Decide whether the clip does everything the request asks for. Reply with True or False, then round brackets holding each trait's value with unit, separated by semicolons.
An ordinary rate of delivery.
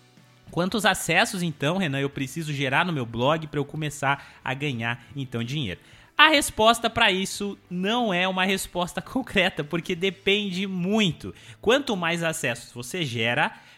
True (150 wpm)